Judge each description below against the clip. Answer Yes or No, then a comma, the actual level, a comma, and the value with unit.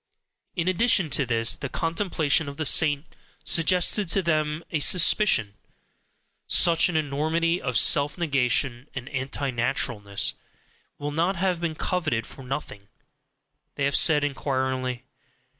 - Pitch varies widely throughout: No, average, 4.3 semitones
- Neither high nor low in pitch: Yes, medium, 145 Hz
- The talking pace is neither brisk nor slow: No, slow, 130 wpm